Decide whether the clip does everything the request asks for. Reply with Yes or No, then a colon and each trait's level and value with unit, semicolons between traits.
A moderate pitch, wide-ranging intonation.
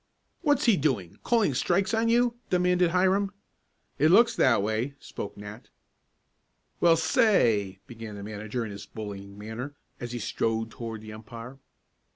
No: low, 120 Hz; wide, 8.9 semitones